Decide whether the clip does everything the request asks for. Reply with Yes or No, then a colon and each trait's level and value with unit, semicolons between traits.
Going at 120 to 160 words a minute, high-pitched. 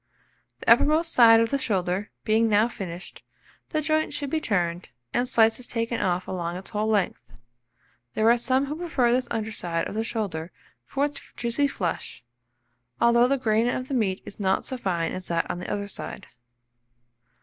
No: average, 180 wpm; high, 225 Hz